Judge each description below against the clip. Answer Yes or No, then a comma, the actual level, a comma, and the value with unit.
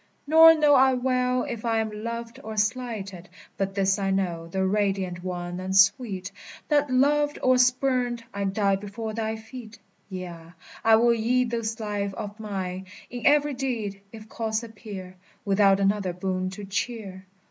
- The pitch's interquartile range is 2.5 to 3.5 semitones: No, average, 4.0 semitones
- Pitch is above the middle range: Yes, high, 215 Hz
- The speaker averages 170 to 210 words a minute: No, average, 160 wpm